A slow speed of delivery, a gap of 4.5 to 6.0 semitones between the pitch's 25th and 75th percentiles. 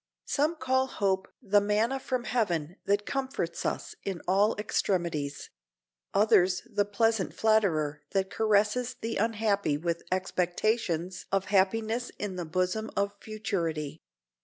No: slow, 125 wpm; average, 3.6 semitones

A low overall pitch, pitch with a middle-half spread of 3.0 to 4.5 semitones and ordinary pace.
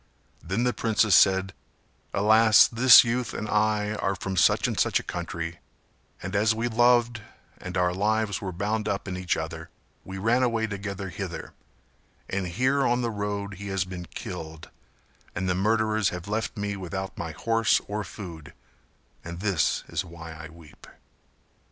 Yes: low, 100 Hz; average, 3.4 semitones; average, 165 wpm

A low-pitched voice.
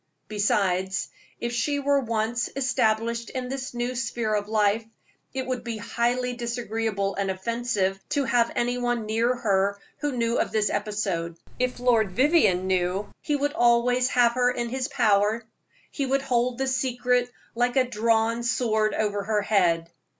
No: high, 235 Hz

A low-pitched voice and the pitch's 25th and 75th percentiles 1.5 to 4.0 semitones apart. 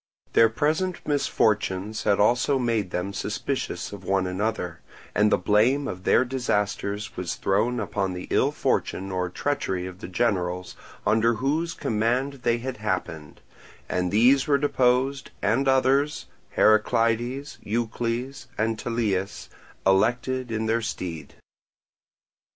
No: low, 115 Hz; average, 4.7 semitones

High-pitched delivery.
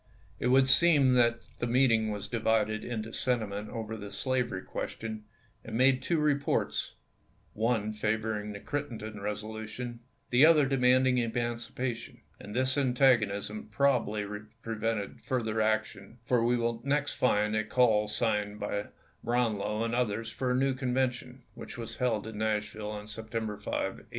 No: low, 115 Hz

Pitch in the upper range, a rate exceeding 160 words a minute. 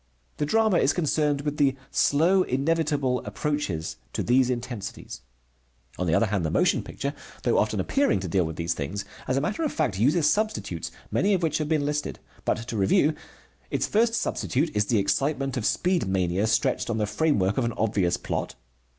No: low, 135 Hz; average, 190 wpm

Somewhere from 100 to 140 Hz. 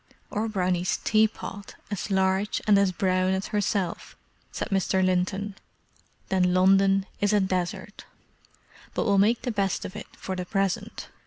No: high, 195 Hz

